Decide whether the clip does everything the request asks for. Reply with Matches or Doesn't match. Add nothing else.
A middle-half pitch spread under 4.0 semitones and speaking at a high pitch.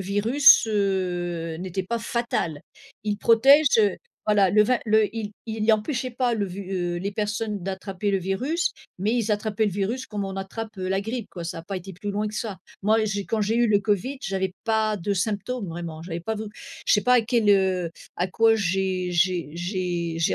Matches